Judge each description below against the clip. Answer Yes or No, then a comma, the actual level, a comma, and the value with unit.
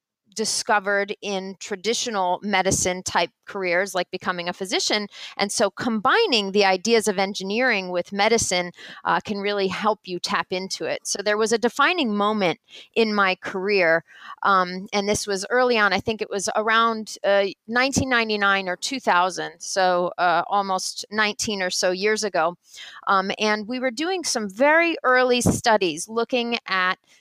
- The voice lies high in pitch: Yes, high, 200 Hz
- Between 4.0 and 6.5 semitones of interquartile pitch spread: No, average, 3.4 semitones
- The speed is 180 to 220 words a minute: No, average, 155 wpm